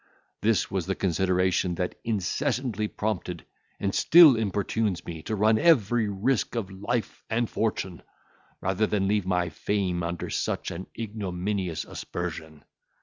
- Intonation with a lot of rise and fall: No, average, 3.5 semitones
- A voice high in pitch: No, low, 100 Hz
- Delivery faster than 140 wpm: No, slow, 135 wpm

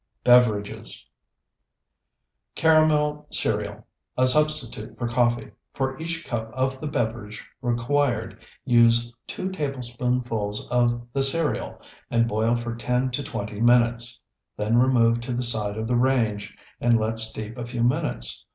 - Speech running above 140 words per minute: No, slow, 135 wpm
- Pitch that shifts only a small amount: Yes, narrow, 2.3 semitones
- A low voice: Yes, low, 120 Hz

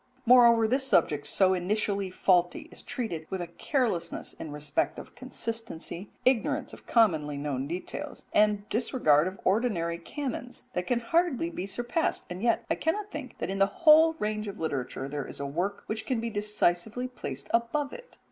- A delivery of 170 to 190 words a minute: Yes, average, 175 wpm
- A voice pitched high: Yes, high, 210 Hz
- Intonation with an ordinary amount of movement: No, wide, 6.2 semitones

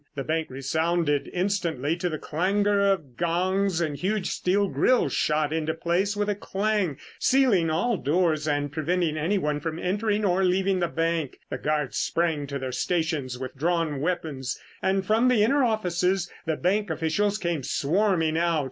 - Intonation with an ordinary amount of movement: Yes, average, 4.1 semitones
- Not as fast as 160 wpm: No, average, 165 wpm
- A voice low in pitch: No, medium, 170 Hz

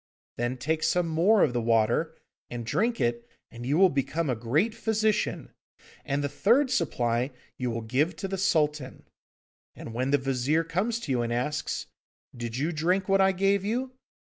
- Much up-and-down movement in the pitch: Yes, wide, 7.9 semitones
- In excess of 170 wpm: Yes, average, 180 wpm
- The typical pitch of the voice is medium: Yes, medium, 150 Hz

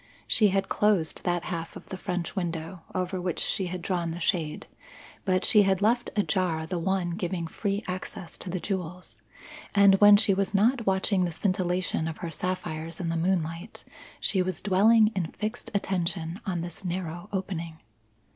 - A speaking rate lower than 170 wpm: No, average, 175 wpm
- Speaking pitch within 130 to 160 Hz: No, medium, 185 Hz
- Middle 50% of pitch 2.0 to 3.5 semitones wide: Yes, narrow, 2.5 semitones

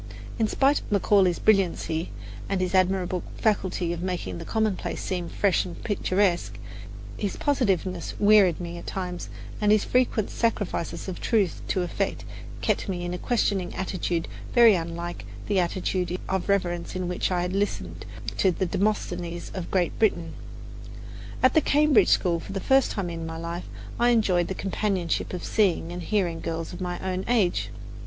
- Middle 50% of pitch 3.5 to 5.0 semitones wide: No, average, 2.9 semitones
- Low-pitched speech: No, medium, 185 Hz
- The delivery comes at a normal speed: Yes, average, 170 wpm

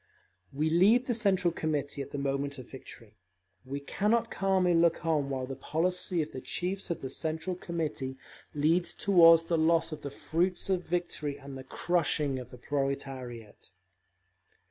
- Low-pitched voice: No, medium, 155 Hz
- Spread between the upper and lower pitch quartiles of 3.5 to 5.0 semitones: Yes, average, 4.3 semitones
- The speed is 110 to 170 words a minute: Yes, average, 165 wpm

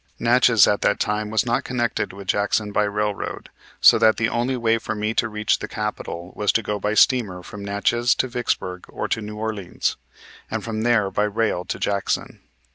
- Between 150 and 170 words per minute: No, average, 200 wpm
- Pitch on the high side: No, low, 105 Hz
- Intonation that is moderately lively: No, narrow, 2.0 semitones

